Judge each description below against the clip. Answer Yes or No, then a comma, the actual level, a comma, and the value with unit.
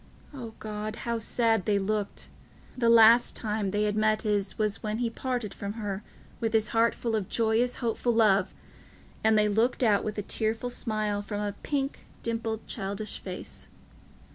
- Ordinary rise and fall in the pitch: No, narrow, 1.8 semitones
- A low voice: No, high, 215 Hz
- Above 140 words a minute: Yes, average, 170 wpm